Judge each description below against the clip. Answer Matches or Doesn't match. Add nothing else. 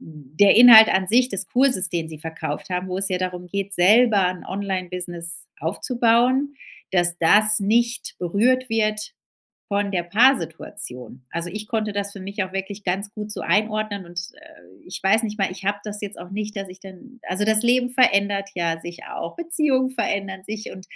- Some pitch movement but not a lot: Matches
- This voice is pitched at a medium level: Doesn't match